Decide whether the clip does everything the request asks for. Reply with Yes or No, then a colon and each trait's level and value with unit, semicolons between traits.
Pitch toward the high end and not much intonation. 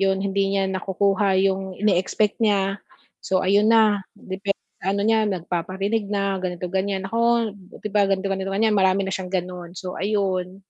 Yes: high, 195 Hz; narrow, 1.2 semitones